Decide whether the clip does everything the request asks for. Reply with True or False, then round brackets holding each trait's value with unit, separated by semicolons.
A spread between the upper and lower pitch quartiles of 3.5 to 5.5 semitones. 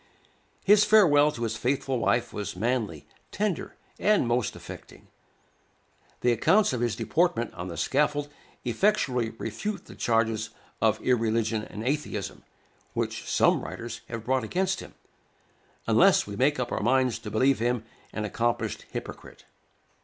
True (4.5 semitones)